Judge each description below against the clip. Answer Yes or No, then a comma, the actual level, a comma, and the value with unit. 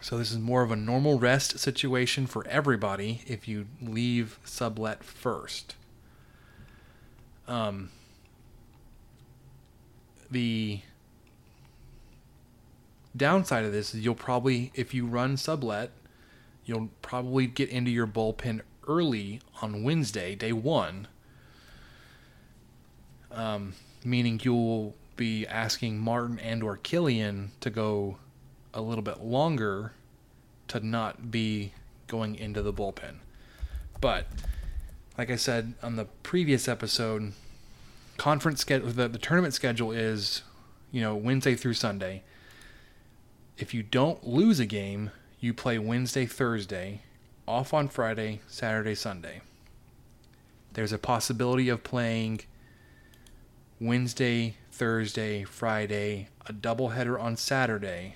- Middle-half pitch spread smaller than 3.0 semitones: Yes, narrow, 2.5 semitones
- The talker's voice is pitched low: Yes, low, 115 Hz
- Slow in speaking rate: Yes, slow, 110 wpm